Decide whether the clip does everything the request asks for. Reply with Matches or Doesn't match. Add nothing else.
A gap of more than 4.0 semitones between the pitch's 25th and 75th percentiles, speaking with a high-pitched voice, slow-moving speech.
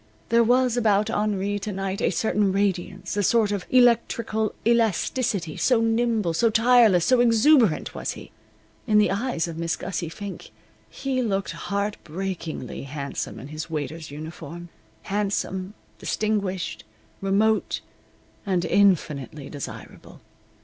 Matches